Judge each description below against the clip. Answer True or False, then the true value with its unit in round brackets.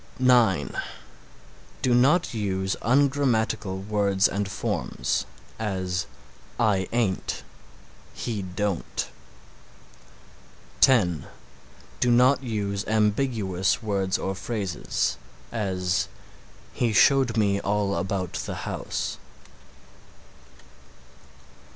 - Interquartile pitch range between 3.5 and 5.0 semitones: True (3.9 semitones)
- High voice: False (105 Hz)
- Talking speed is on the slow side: True (80 wpm)